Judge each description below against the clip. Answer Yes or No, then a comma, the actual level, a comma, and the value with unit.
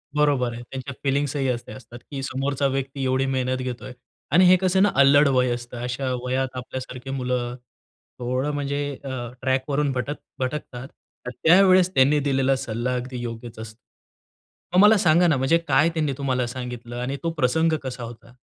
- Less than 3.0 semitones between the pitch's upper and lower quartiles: Yes, narrow, 2.4 semitones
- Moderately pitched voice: No, low, 130 Hz